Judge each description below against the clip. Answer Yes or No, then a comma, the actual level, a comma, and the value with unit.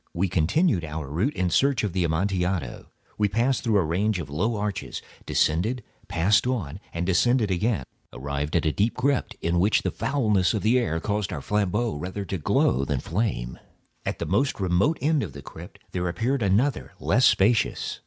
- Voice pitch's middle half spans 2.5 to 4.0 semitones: No, wide, 5.4 semitones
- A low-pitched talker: Yes, very low, 95 Hz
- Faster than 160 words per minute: Yes, average, 185 wpm